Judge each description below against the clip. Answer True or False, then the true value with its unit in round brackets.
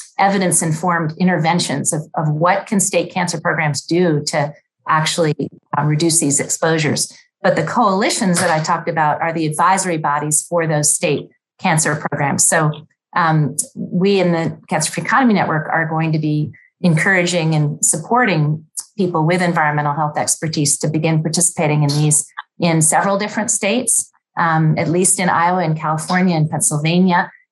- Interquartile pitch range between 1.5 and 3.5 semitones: True (2.8 semitones)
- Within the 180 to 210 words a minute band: False (155 wpm)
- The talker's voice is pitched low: False (165 Hz)